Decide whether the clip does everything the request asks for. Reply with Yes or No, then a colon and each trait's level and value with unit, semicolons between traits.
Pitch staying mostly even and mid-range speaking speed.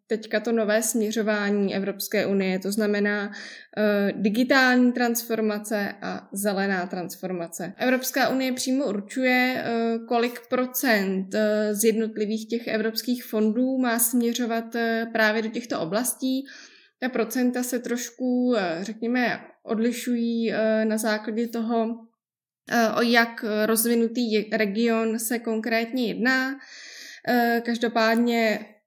No: narrow, 2.2 semitones; slow, 100 wpm